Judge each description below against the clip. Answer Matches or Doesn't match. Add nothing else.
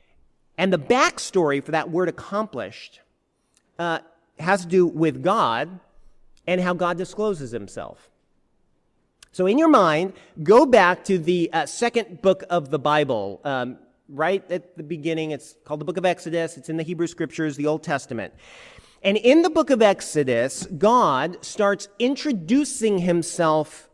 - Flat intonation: Doesn't match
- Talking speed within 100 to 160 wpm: Matches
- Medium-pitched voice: Matches